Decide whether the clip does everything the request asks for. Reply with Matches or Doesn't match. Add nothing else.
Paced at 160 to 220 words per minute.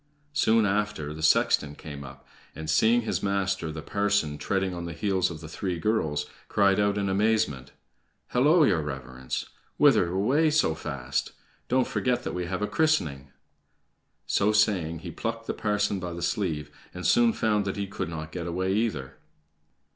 Matches